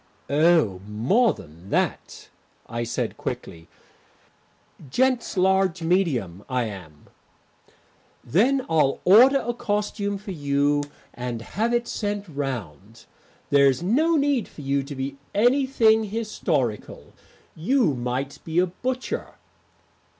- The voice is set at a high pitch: No, medium, 165 Hz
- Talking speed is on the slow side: Yes, slow, 115 wpm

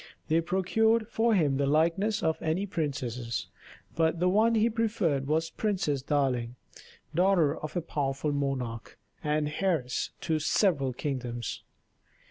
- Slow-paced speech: Yes, slow, 130 wpm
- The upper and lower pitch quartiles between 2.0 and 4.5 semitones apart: No, wide, 5.6 semitones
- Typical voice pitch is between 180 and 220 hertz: No, medium, 155 Hz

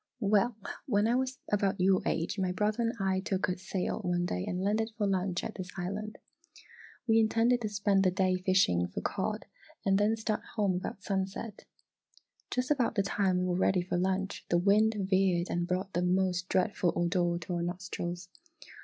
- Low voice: No, high, 190 Hz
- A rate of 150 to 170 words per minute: No, average, 190 wpm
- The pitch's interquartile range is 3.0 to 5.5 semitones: No, narrow, 2.6 semitones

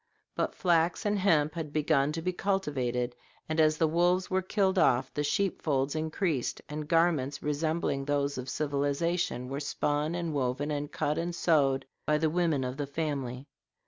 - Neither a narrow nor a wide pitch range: Yes, average, 3.2 semitones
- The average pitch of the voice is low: No, medium, 150 Hz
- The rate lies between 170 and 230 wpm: Yes, average, 175 wpm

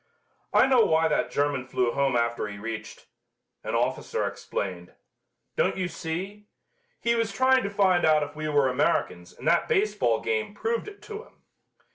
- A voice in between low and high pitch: Yes, medium, 160 Hz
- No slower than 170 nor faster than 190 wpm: Yes, average, 175 wpm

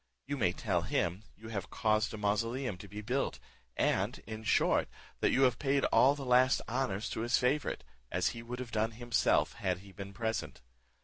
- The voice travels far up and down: No, average, 3.5 semitones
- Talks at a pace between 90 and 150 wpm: No, average, 195 wpm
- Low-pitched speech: Yes, low, 115 Hz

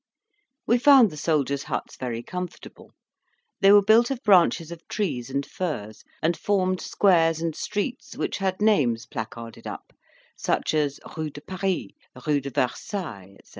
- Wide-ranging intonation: Yes, wide, 6.2 semitones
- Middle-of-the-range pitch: Yes, medium, 165 Hz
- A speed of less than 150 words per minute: No, average, 155 wpm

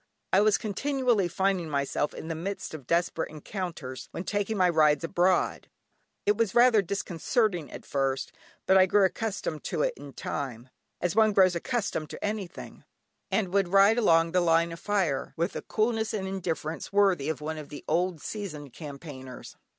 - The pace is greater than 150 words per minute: Yes, average, 175 wpm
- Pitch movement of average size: Yes, average, 4.6 semitones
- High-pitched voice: No, medium, 180 Hz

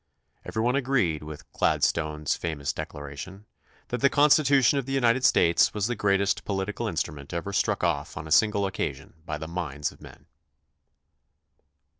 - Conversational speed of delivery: Yes, average, 160 wpm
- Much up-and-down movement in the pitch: Yes, wide, 7.7 semitones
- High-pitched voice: No, very low, 95 Hz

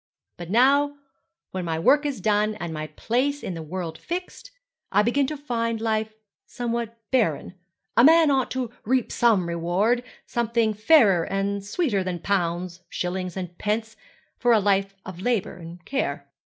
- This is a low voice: No, high, 215 Hz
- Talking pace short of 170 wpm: Yes, average, 160 wpm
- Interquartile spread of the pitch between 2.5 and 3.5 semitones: No, average, 5.1 semitones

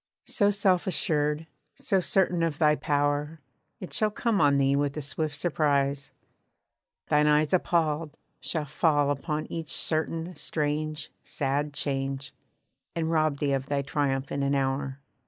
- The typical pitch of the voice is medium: Yes, medium, 150 Hz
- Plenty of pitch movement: No, narrow, 2.5 semitones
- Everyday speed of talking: Yes, average, 145 wpm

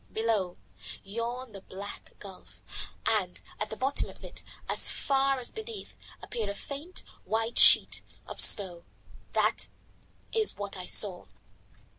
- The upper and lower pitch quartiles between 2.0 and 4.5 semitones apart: No, average, 5.2 semitones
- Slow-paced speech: Yes, slow, 130 wpm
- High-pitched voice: Yes, high, 220 Hz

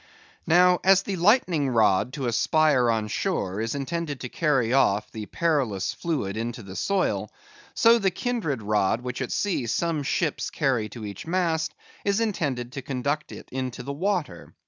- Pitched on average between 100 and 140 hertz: Yes, low, 135 Hz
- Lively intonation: Yes, wide, 6.8 semitones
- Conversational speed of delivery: Yes, average, 170 wpm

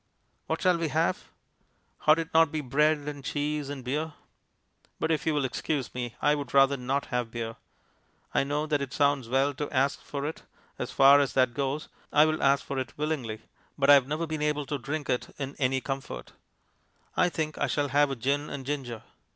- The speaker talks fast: Yes, fast, 210 wpm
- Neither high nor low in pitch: Yes, medium, 145 Hz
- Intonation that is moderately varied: No, narrow, 2.1 semitones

